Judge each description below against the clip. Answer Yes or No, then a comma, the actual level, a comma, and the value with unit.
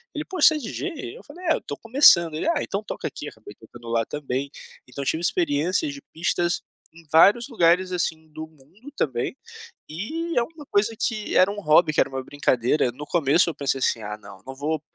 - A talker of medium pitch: Yes, medium, 165 Hz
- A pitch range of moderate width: No, wide, 8.4 semitones